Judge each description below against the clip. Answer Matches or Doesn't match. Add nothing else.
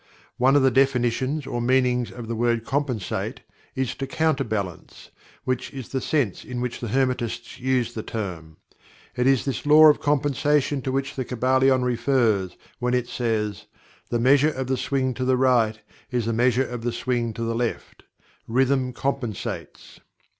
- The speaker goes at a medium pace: Matches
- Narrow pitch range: Matches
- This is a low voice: Matches